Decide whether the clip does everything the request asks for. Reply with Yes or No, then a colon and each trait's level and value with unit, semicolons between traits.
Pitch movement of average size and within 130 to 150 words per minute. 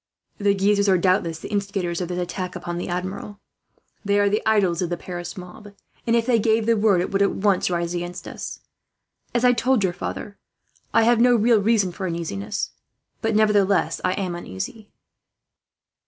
No: average, 3.3 semitones; average, 185 wpm